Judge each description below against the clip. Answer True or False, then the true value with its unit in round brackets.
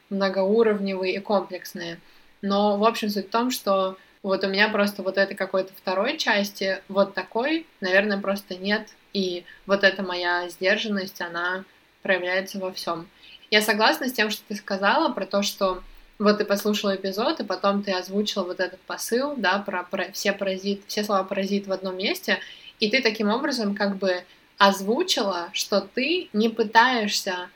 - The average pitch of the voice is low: False (200 Hz)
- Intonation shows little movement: True (2.0 semitones)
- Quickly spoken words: True (165 wpm)